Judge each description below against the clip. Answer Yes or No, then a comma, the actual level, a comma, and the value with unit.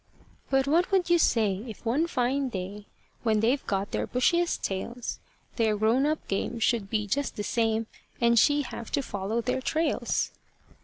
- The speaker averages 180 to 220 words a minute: No, average, 170 wpm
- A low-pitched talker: No, high, 235 Hz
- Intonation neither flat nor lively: Yes, average, 4.7 semitones